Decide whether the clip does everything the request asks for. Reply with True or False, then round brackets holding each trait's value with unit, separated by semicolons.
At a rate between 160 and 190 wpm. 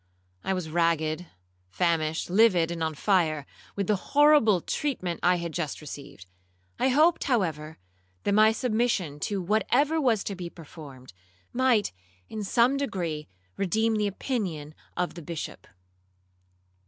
False (135 wpm)